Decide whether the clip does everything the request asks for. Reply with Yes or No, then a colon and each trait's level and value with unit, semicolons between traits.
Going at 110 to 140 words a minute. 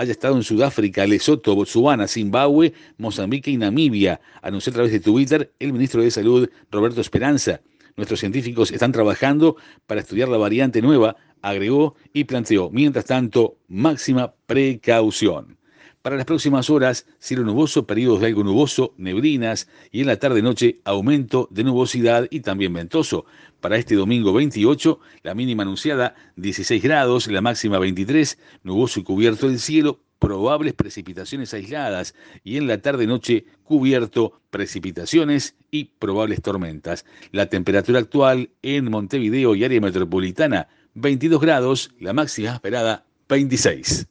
Yes: average, 135 wpm